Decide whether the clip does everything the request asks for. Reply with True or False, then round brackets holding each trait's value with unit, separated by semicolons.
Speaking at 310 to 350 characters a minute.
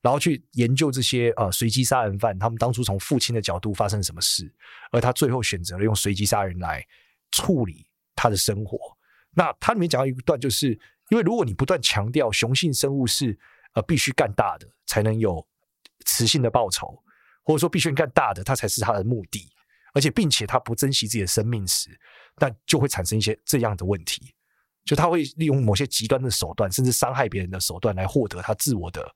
True (315 characters per minute)